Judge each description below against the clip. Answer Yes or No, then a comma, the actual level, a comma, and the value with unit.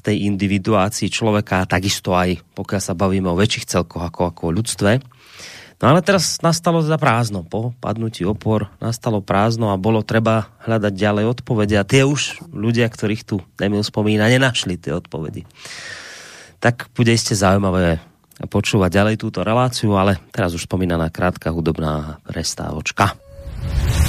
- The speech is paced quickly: No, average, 145 wpm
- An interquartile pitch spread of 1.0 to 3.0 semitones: No, average, 3.6 semitones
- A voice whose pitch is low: Yes, low, 105 Hz